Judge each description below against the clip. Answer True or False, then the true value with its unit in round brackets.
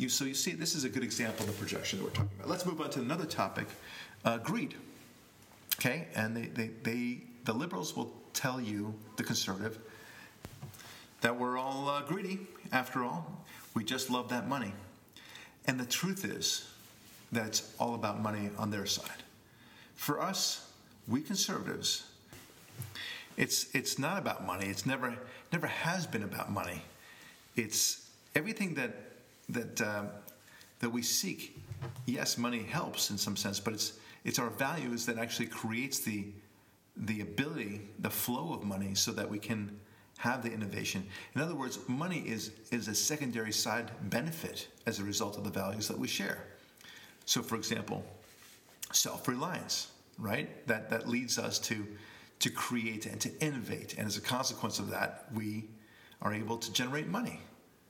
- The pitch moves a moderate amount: True (3.4 semitones)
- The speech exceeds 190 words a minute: False (165 wpm)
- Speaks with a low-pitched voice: True (115 Hz)